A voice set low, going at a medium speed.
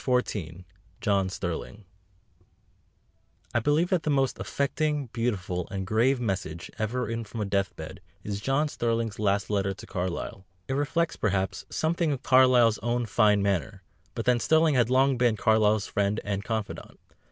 Yes: low, 110 Hz; average, 155 wpm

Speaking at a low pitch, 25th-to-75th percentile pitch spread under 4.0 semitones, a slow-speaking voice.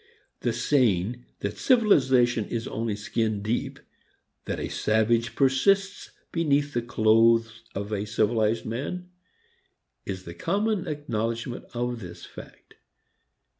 No: low, 115 Hz; average, 4.3 semitones; slow, 115 wpm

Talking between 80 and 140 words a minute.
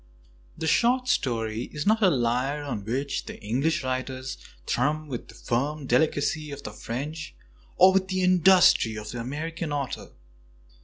No: average, 155 wpm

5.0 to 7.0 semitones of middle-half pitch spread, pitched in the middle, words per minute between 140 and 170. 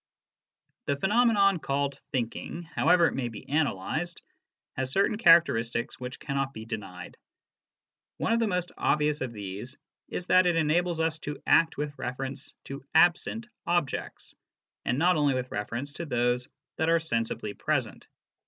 Yes: wide, 5.5 semitones; medium, 145 Hz; average, 150 wpm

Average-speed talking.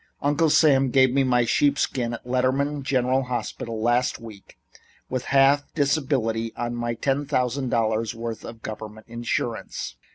Yes: average, 150 wpm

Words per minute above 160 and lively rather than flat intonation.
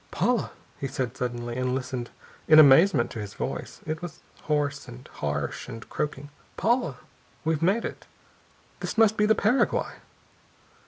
No: average, 150 wpm; wide, 6.5 semitones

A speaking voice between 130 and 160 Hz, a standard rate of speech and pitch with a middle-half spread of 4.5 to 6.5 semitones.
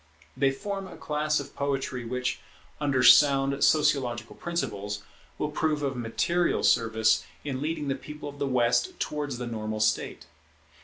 No: low, 135 Hz; average, 150 wpm; average, 3.8 semitones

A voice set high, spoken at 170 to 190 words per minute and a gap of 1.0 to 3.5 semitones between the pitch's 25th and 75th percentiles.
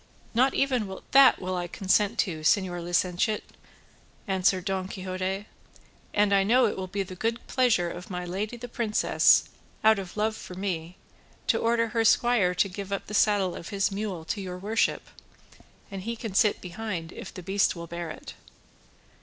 Yes: high, 195 Hz; average, 180 wpm; average, 3.1 semitones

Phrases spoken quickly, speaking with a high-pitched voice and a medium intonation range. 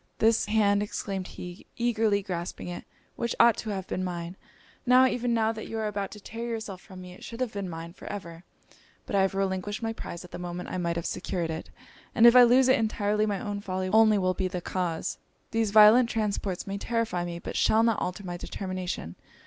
Yes: fast, 220 wpm; high, 200 Hz; average, 3.7 semitones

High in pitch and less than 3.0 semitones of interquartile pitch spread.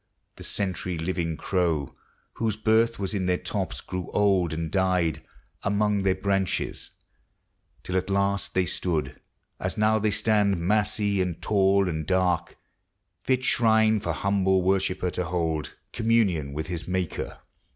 No: very low, 95 Hz; narrow, 2.6 semitones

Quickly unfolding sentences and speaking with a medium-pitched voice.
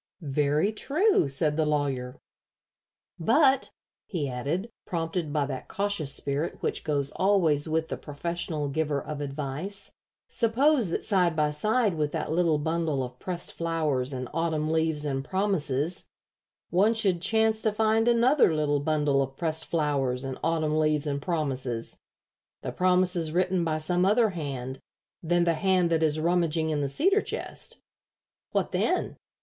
No: average, 150 wpm; medium, 160 Hz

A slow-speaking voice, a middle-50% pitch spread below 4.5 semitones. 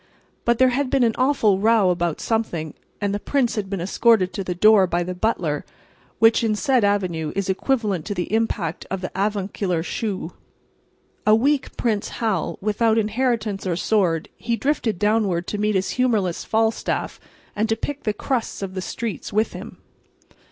No: average, 175 wpm; average, 3.5 semitones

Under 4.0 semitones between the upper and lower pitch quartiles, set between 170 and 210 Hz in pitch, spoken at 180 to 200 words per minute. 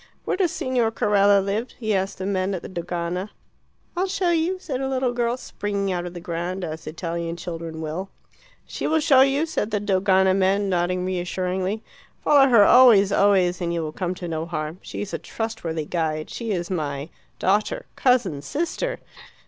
No: average, 5.1 semitones; high, 190 Hz; average, 185 wpm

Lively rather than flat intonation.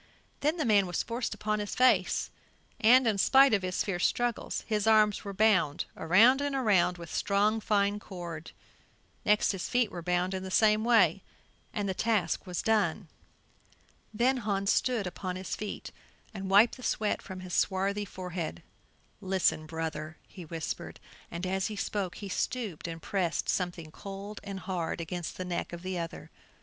No: average, 3.3 semitones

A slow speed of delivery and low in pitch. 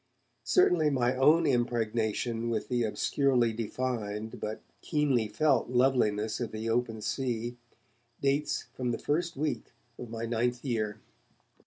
Yes: slow, 130 wpm; low, 120 Hz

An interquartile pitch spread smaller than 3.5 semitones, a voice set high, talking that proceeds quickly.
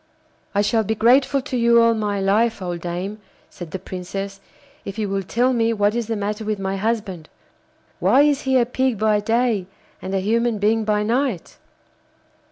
No: average, 3.1 semitones; high, 215 Hz; average, 185 wpm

